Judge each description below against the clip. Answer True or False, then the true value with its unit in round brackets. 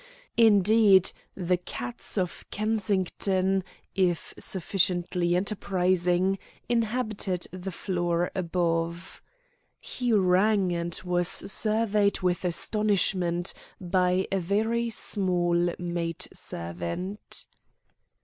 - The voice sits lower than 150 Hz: False (185 Hz)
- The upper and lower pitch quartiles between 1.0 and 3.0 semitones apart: True (2.5 semitones)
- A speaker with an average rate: False (80 wpm)